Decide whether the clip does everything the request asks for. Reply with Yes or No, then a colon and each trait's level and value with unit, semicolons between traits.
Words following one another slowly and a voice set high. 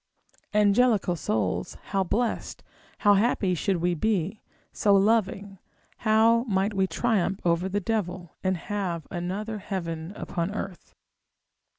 Yes: slow, 120 wpm; high, 195 Hz